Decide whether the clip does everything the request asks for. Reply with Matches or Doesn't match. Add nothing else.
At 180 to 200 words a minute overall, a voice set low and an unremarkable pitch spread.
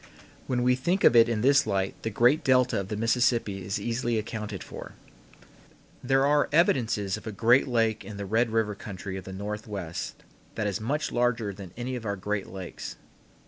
Matches